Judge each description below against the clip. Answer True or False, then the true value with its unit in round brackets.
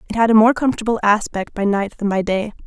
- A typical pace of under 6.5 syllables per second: False (6.6 syllables/s)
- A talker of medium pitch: False (215 Hz)